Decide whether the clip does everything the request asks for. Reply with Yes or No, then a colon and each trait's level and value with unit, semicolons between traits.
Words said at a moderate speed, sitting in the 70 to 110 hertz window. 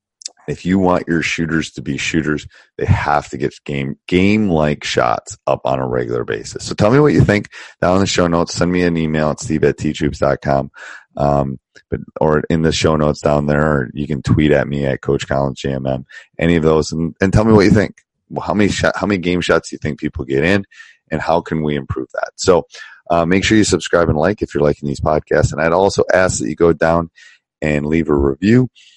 No: fast, 230 wpm; very low, 80 Hz